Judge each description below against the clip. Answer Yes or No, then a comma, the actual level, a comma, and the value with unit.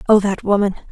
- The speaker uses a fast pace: No, average, 195 wpm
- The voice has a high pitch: Yes, high, 200 Hz